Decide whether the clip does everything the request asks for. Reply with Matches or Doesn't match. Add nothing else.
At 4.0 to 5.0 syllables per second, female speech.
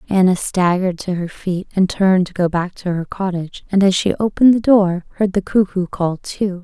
Doesn't match